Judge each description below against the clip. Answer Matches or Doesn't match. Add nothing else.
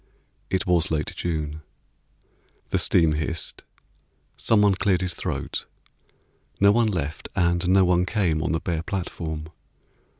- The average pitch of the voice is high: Doesn't match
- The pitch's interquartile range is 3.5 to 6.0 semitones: Doesn't match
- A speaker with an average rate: Doesn't match